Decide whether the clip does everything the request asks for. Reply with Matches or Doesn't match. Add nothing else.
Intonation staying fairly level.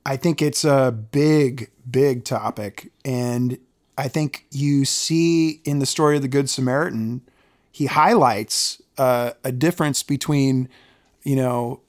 Matches